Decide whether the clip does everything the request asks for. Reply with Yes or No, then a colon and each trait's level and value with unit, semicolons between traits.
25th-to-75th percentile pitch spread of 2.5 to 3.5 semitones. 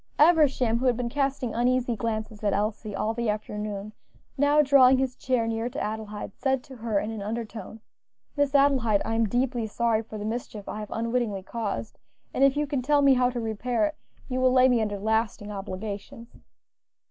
Yes: average, 3.2 semitones